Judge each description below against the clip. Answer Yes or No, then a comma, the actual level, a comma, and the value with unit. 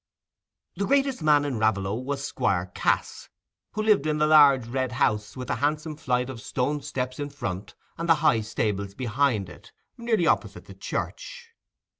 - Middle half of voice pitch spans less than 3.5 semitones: No, wide, 5.6 semitones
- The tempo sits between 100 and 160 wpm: No, average, 170 wpm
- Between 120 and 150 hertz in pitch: Yes, low, 135 Hz